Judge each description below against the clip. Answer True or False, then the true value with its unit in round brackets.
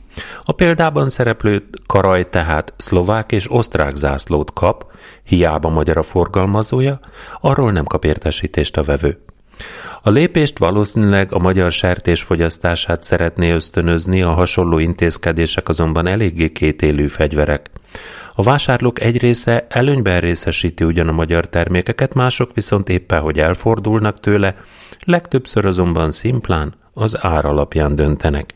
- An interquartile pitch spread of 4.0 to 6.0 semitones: True (5.0 semitones)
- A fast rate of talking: False (125 wpm)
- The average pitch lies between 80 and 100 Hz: True (90 Hz)